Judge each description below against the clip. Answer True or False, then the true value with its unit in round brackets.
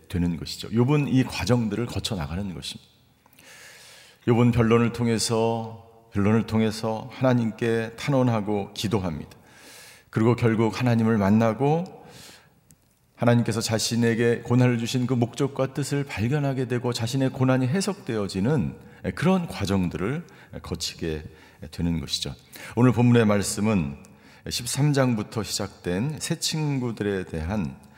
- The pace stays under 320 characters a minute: True (285 characters per minute)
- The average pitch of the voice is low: True (115 Hz)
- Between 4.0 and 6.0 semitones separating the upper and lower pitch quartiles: False (3.6 semitones)